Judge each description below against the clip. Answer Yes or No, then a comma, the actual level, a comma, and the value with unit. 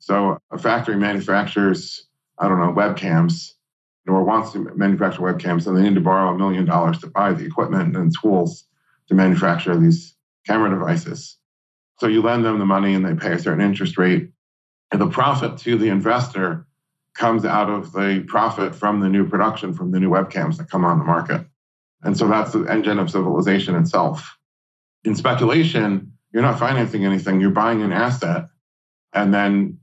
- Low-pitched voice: Yes, low, 105 Hz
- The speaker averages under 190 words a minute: Yes, average, 180 wpm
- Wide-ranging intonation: Yes, wide, 7.1 semitones